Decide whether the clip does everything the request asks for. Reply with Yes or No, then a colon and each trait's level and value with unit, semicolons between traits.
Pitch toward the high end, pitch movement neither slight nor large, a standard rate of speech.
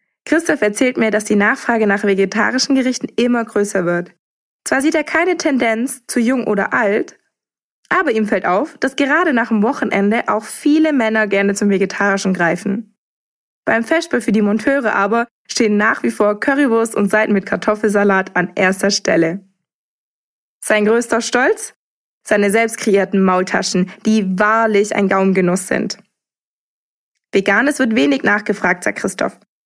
Yes: high, 215 Hz; average, 3.5 semitones; average, 150 wpm